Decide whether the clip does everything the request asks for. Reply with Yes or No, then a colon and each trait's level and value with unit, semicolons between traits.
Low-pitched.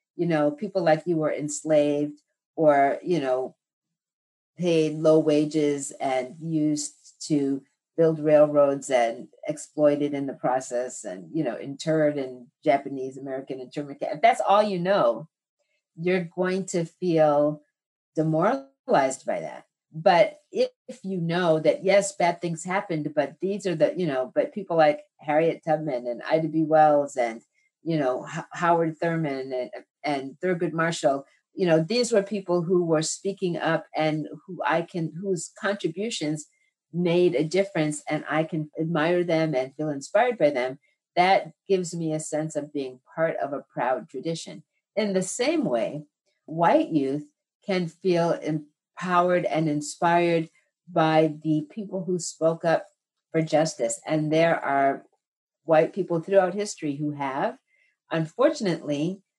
No: medium, 160 Hz